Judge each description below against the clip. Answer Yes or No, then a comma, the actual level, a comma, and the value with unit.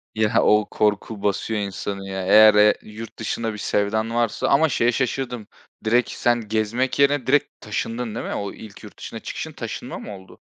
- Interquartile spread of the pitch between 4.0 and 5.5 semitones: No, narrow, 2.5 semitones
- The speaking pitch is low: Yes, low, 110 Hz